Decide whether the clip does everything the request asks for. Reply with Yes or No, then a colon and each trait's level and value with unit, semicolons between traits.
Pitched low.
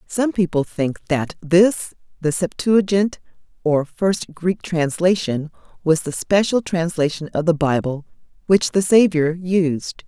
No: medium, 170 Hz